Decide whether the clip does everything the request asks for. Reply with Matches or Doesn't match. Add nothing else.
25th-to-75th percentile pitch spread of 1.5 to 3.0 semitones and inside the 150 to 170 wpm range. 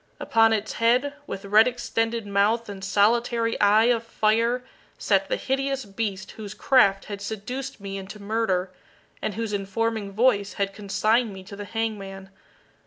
Matches